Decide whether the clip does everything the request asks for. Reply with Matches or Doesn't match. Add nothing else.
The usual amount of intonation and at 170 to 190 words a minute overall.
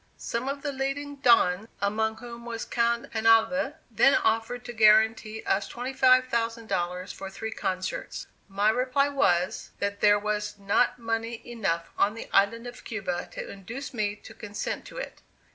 Doesn't match